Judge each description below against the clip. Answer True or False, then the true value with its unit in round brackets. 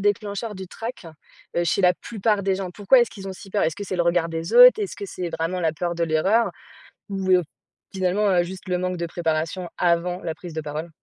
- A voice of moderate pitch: True (180 Hz)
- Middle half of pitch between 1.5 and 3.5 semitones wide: True (2.8 semitones)